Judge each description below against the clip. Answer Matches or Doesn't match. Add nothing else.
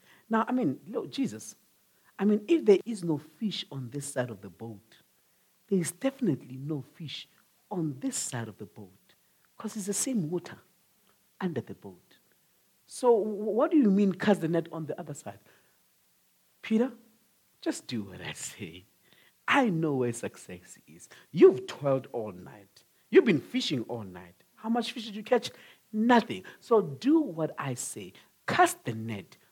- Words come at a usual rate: Matches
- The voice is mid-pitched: Matches